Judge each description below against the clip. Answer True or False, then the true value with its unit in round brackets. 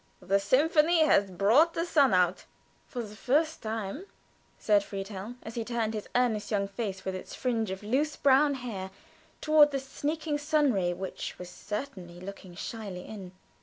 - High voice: True (220 Hz)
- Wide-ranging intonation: True (6.5 semitones)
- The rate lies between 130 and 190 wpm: True (165 wpm)